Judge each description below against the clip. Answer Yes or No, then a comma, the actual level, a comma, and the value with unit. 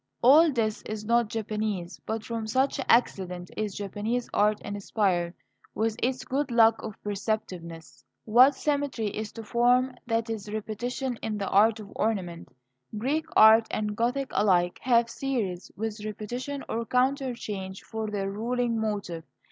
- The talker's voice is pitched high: Yes, high, 220 Hz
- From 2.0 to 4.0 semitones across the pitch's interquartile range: Yes, average, 2.9 semitones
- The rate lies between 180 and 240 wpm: No, average, 150 wpm